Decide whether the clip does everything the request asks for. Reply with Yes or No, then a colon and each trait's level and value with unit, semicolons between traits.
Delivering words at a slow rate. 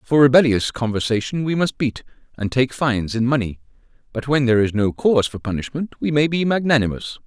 No: average, 190 wpm